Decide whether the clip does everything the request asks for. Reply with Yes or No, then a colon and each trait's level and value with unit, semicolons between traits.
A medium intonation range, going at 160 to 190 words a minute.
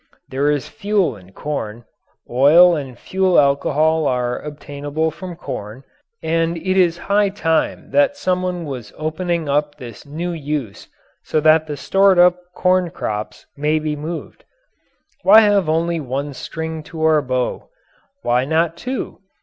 No: average, 3.8 semitones; average, 145 wpm